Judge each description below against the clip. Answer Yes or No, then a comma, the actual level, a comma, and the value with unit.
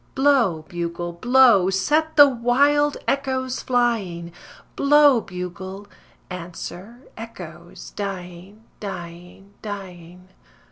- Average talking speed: No, slow, 85 wpm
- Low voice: No, high, 200 Hz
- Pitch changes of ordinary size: No, wide, 6.5 semitones